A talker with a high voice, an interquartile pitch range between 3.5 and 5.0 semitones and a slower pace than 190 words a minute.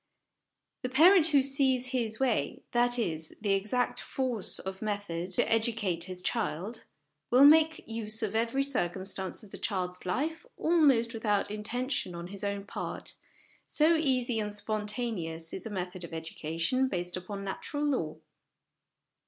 No: high, 215 Hz; wide, 5.4 semitones; average, 150 wpm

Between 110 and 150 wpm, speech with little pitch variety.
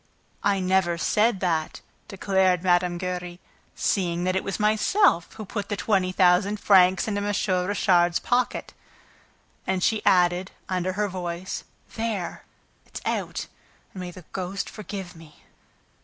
Yes: average, 140 wpm; narrow, 2.2 semitones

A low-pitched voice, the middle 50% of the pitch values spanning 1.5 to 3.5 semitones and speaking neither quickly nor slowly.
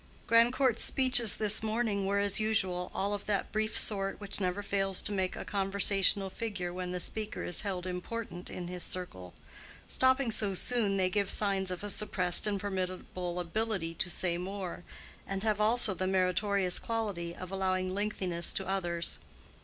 No: high, 195 Hz; narrow, 2.6 semitones; average, 170 wpm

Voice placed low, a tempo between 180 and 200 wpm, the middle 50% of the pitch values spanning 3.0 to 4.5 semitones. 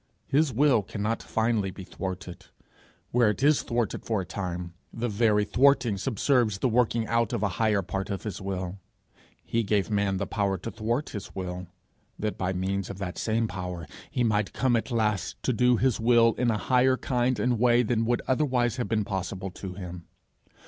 Yes: low, 110 Hz; average, 190 wpm; average, 3.8 semitones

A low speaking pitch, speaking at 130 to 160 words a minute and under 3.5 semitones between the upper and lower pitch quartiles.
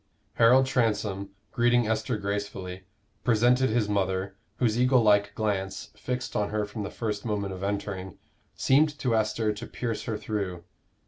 Yes: low, 105 Hz; average, 150 wpm; average, 2.9 semitones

